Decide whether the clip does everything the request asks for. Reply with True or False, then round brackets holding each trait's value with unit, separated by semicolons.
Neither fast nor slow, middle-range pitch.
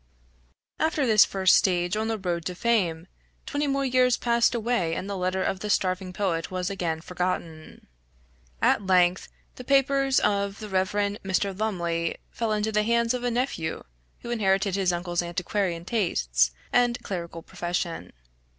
False (160 wpm; 195 Hz)